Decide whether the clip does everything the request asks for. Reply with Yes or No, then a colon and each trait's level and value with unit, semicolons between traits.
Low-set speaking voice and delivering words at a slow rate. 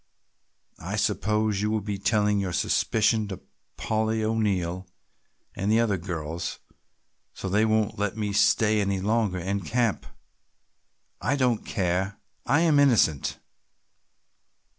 Yes: low, 105 Hz; slow, 125 wpm